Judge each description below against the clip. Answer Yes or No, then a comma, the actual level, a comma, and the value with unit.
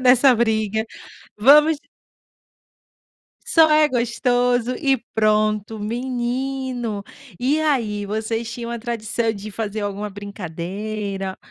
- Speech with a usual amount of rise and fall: Yes, average, 3.2 semitones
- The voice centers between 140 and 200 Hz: No, high, 225 Hz